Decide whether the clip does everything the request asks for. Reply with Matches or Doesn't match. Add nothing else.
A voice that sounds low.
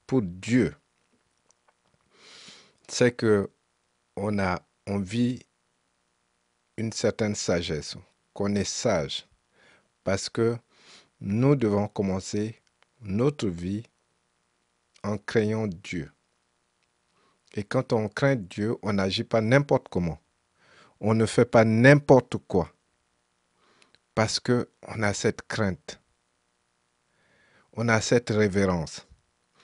Matches